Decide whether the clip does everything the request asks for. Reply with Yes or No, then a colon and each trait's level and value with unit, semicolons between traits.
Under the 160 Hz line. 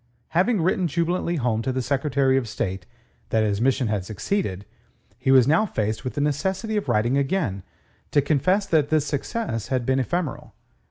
Yes: low, 135 Hz